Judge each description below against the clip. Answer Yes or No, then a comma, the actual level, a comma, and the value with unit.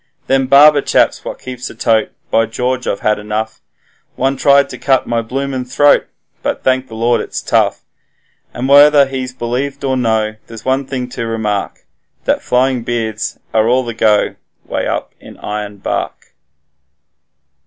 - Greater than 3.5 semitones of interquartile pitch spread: No, average, 3.1 semitones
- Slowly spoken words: No, average, 160 wpm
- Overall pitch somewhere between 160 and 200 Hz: No, low, 125 Hz